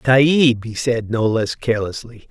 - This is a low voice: Yes, low, 120 Hz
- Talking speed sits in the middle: Yes, average, 155 wpm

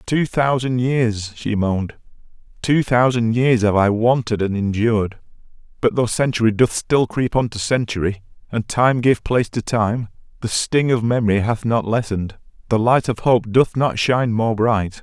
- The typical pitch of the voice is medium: No, low, 115 Hz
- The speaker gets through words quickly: No, average, 170 wpm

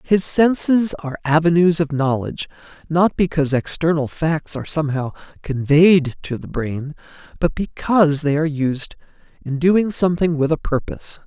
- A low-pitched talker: No, medium, 155 Hz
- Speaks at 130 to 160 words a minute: Yes, average, 145 wpm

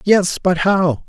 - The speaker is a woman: No, male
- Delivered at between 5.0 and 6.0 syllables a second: No, 3.2 syllables/s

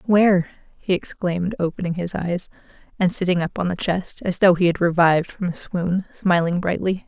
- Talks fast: No, average, 185 wpm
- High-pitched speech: No, medium, 180 Hz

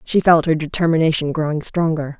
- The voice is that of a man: No, female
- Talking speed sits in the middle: Yes, average, 165 wpm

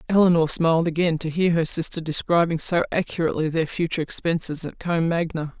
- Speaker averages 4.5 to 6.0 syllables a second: No, 6.2 syllables/s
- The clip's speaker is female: Yes, female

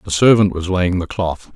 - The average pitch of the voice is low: Yes, very low, 95 Hz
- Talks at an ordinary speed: No, fast, 230 wpm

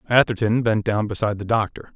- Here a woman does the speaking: No, male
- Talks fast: No, average, 185 wpm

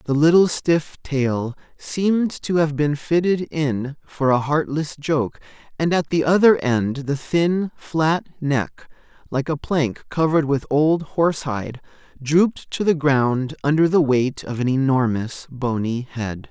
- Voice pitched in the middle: Yes, medium, 145 Hz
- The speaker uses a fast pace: No, average, 155 wpm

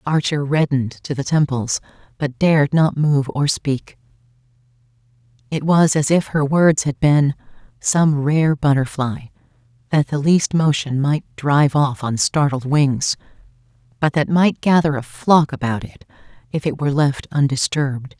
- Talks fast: No, average, 150 wpm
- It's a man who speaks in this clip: No, female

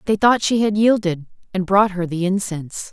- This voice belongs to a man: No, female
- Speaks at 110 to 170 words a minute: No, fast, 205 wpm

